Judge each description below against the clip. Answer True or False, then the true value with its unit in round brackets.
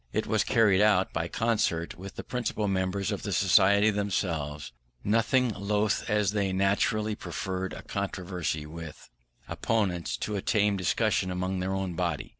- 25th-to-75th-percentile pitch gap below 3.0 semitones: True (2.4 semitones)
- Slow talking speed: False (155 wpm)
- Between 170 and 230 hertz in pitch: False (95 Hz)